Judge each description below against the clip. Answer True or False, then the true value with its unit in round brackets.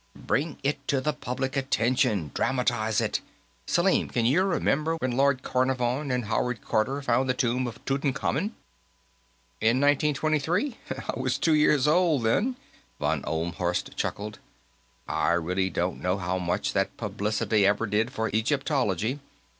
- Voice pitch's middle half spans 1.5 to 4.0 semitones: False (4.6 semitones)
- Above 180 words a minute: False (140 wpm)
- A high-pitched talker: False (130 Hz)